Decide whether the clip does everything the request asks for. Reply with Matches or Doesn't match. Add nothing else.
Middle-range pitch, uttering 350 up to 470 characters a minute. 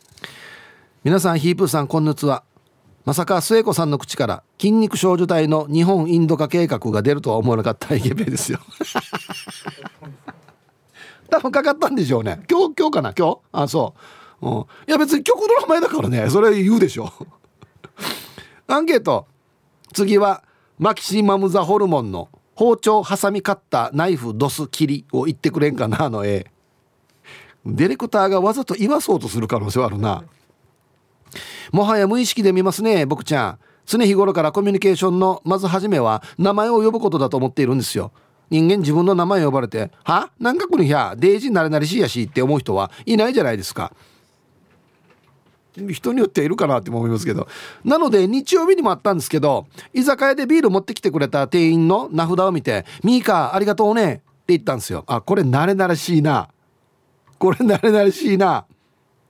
Matches